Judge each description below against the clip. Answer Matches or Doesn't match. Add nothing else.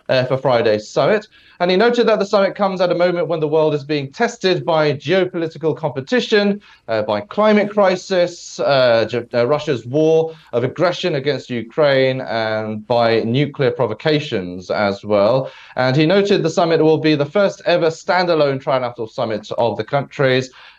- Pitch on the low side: Doesn't match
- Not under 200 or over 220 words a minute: Doesn't match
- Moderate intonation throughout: Doesn't match